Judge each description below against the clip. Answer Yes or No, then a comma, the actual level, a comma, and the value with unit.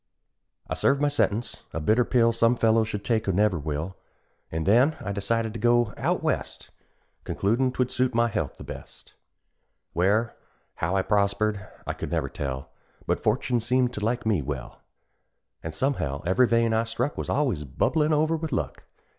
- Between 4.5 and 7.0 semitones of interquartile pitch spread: No, average, 4.1 semitones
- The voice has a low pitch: Yes, low, 115 Hz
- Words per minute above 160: Yes, average, 180 wpm